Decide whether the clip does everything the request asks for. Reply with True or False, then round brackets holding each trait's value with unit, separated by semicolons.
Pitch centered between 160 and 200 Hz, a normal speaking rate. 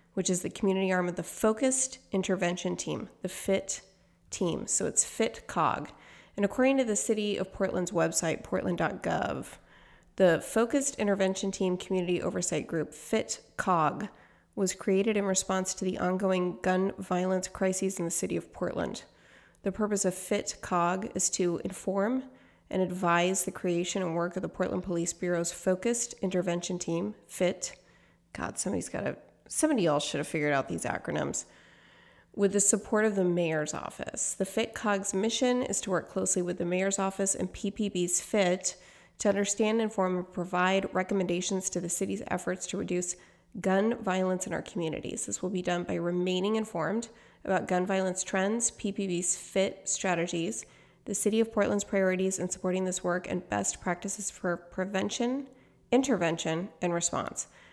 True (185 Hz; 160 wpm)